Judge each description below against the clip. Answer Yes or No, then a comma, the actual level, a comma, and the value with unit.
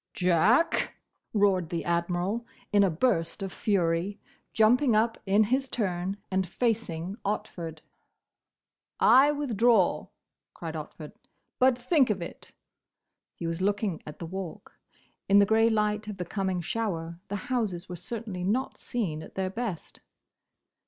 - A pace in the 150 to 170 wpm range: No, average, 140 wpm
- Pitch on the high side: Yes, high, 200 Hz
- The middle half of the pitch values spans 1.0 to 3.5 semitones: No, average, 4.3 semitones